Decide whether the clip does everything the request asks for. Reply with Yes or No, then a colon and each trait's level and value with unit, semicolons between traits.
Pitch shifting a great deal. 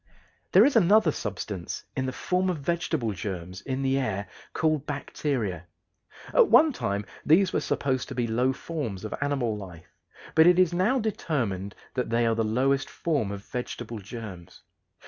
Yes: wide, 7.4 semitones